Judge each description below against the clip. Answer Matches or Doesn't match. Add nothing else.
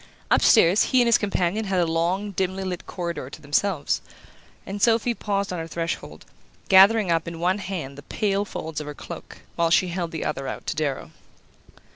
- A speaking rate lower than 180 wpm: Doesn't match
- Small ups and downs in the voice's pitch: Doesn't match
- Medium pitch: Matches